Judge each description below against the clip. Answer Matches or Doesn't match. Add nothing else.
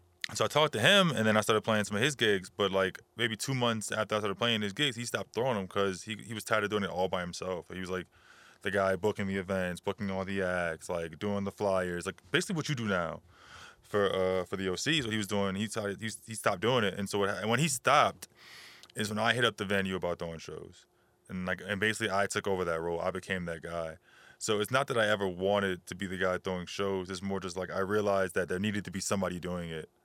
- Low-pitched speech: Matches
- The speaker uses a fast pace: Matches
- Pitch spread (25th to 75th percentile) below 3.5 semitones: Matches